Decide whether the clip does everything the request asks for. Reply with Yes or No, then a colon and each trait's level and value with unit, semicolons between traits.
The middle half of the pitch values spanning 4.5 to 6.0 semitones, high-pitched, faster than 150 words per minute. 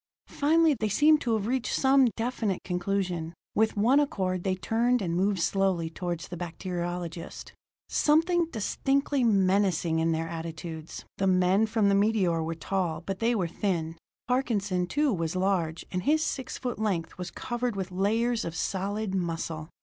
Yes: average, 5.1 semitones; high, 195 Hz; average, 160 wpm